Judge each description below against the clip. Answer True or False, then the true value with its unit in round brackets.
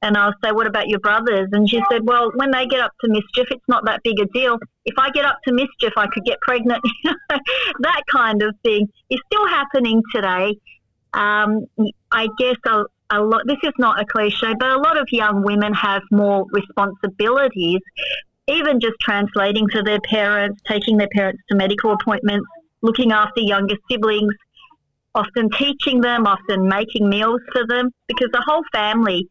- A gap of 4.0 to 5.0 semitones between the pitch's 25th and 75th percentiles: False (3.4 semitones)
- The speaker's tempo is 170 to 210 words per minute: True (180 wpm)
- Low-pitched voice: False (225 Hz)